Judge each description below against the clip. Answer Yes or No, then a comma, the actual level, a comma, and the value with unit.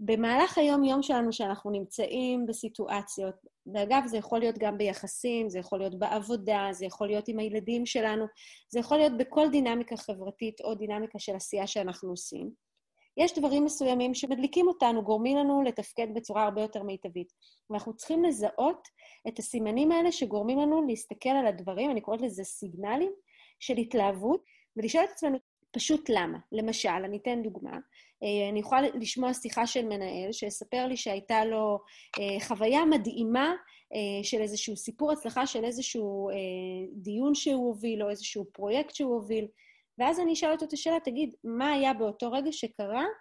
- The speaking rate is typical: No, fast, 155 wpm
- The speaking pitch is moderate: No, high, 230 Hz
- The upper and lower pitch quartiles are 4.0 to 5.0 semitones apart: Yes, average, 4.4 semitones